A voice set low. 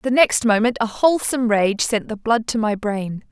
No: high, 225 Hz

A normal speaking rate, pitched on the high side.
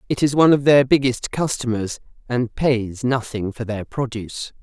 No: average, 170 wpm; low, 125 Hz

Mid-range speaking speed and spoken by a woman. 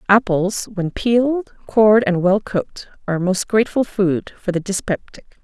Yes: average, 165 wpm; female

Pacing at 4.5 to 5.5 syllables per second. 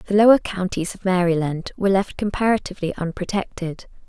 No: 5.8 syllables/s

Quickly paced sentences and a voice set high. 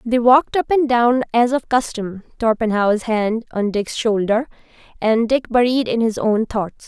No: average, 175 wpm; high, 230 Hz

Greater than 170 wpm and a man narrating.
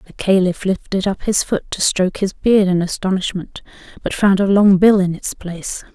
No: average, 200 wpm; female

